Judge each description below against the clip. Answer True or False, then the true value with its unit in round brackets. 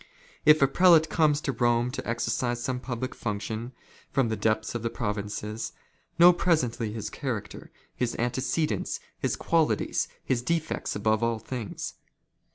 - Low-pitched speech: True (120 Hz)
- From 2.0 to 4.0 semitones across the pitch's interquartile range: False (4.4 semitones)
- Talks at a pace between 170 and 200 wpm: False (155 wpm)